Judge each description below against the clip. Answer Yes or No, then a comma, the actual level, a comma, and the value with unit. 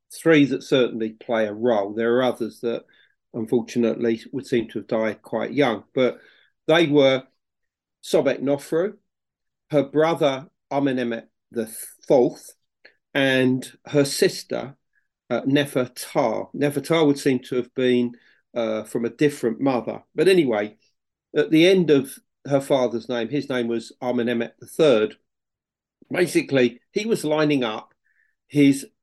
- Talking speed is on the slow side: Yes, slow, 130 wpm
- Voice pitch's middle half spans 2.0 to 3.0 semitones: No, average, 3.5 semitones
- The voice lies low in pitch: Yes, low, 130 Hz